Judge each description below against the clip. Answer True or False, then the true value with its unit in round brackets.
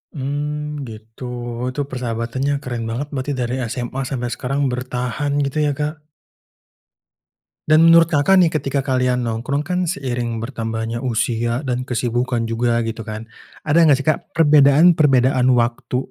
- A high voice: False (130 Hz)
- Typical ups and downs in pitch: True (3.7 semitones)